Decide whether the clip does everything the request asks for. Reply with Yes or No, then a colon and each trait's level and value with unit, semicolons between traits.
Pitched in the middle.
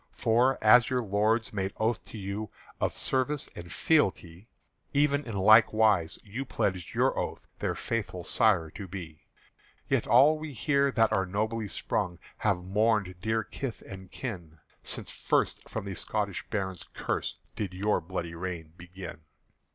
No: low, 105 Hz